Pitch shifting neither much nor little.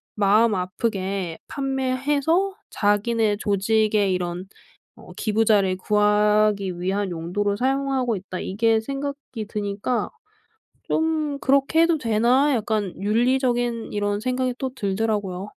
Yes: average, 4.3 semitones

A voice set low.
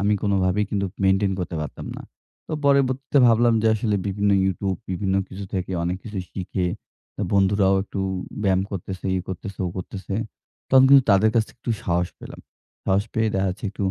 Yes: low, 100 Hz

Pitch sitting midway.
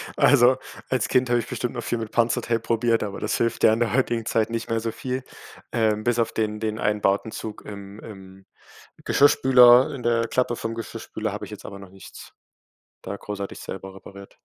No: low, 115 Hz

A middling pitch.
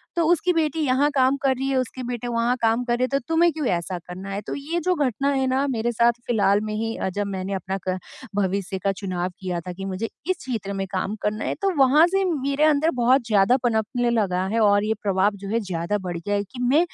No: high, 230 Hz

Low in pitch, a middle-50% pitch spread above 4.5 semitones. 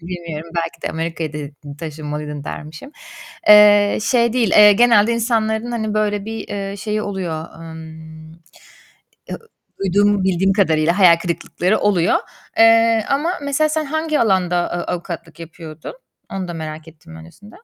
No: high, 190 Hz; average, 5.0 semitones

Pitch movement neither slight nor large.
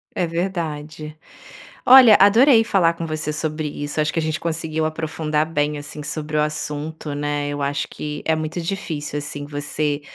No: narrow, 1.9 semitones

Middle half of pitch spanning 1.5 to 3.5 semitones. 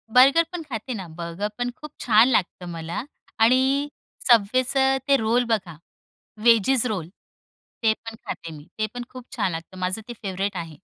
No: average, 5.3 semitones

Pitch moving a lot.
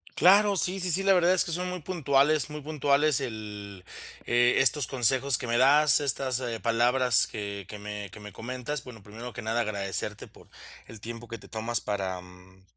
Yes: wide, 5.7 semitones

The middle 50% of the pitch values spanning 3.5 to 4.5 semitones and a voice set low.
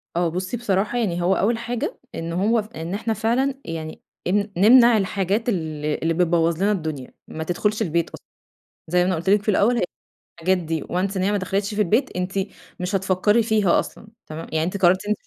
No: average, 3.8 semitones; high, 190 Hz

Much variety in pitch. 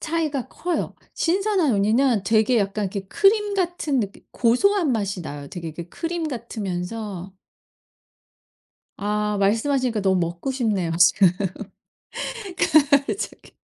Yes: wide, 8.0 semitones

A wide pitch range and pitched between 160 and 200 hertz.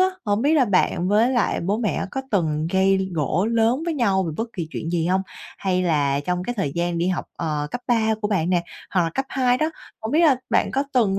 Yes: wide, 5.8 semitones; high, 195 Hz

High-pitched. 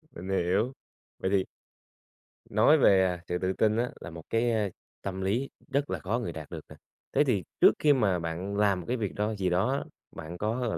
No: low, 100 Hz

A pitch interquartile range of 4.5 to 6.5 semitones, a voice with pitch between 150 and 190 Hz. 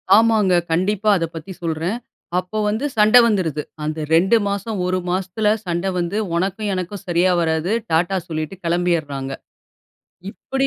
No: average, 3.9 semitones; medium, 185 Hz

